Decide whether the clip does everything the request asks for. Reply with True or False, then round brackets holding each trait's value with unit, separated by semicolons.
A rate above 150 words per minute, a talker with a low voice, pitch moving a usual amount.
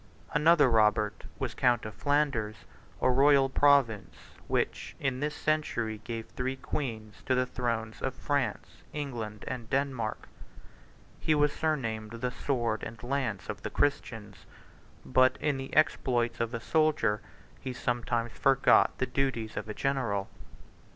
False (140 wpm; 125 Hz; 3.8 semitones)